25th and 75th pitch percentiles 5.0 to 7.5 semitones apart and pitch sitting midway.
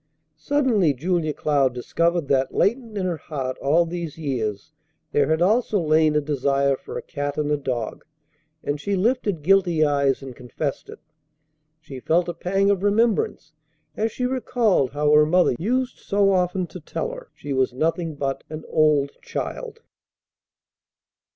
Yes: wide, 5.5 semitones; medium, 160 Hz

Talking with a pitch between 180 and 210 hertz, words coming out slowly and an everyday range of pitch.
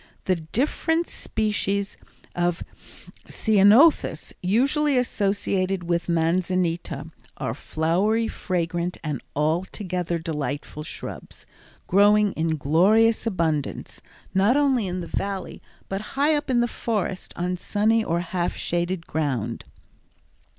Yes: medium, 185 Hz; slow, 110 wpm; average, 4.4 semitones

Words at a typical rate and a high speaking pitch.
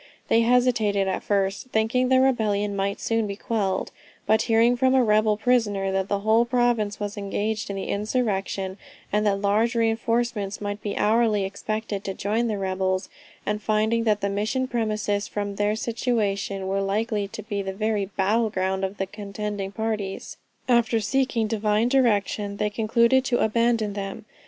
Yes: average, 165 wpm; high, 210 Hz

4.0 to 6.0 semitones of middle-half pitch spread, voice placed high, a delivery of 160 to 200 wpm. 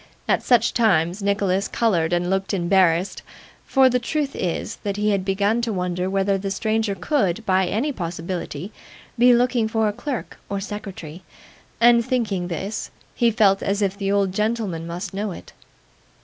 No: average, 3.4 semitones; high, 200 Hz; average, 165 wpm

